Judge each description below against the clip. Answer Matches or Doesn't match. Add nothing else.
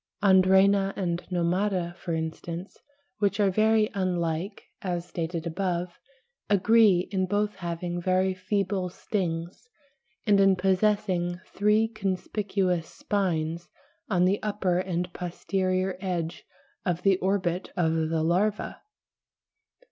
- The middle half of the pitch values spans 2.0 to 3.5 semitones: Matches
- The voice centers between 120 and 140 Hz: Doesn't match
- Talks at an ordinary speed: Doesn't match